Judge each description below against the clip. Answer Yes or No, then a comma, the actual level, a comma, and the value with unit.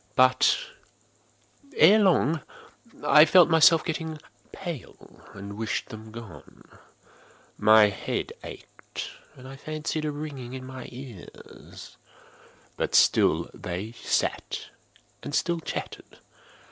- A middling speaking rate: No, slow, 110 wpm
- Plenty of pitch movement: Yes, wide, 5.9 semitones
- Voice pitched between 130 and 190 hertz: Yes, low, 135 Hz